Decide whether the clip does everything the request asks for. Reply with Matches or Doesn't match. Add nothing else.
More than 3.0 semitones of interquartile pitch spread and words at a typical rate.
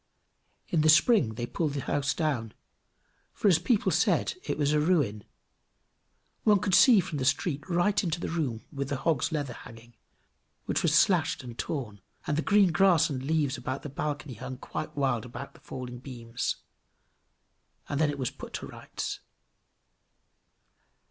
Matches